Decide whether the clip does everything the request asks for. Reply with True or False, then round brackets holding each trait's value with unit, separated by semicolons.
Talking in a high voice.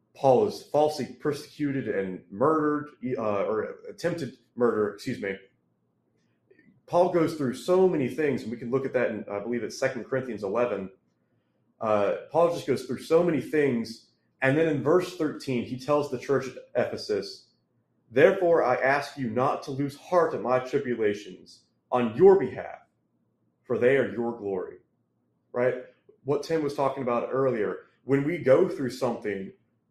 False (135 Hz)